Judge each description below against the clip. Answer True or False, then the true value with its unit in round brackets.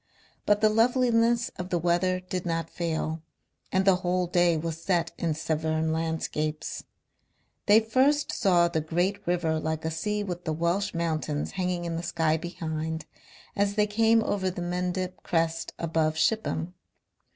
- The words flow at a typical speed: True (155 wpm)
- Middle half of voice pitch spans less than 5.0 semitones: True (3.4 semitones)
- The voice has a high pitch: False (175 Hz)